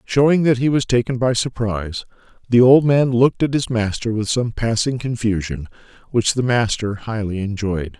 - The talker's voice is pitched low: Yes, low, 115 Hz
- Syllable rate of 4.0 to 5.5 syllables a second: Yes, 5.0 syllables/s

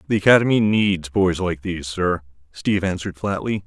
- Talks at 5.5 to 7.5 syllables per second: No, 5.2 syllables/s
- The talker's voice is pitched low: Yes, very low, 95 Hz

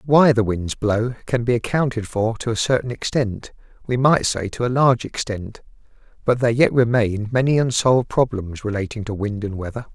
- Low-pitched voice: Yes, low, 115 Hz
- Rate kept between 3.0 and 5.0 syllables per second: No, 5.3 syllables/s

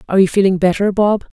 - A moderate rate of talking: No, fast, 215 wpm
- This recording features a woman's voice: Yes, female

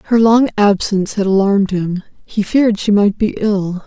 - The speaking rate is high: No, average, 185 wpm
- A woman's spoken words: Yes, female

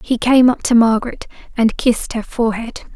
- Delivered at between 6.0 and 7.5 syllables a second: No, 5.6 syllables/s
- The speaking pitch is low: No, high, 235 Hz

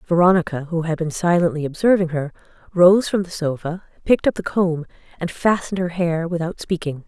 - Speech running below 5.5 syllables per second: No, 5.7 syllables/s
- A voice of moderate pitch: Yes, medium, 170 Hz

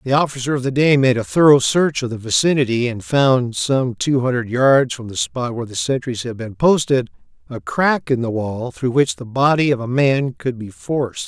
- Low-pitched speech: Yes, low, 130 Hz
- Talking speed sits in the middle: No, fast, 225 wpm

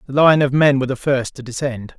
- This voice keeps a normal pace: No, fast, 240 wpm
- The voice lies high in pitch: No, low, 135 Hz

